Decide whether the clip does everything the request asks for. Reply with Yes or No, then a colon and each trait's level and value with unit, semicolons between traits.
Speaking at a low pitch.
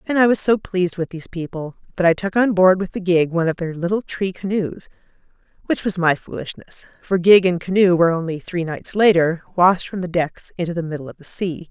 No: medium, 180 Hz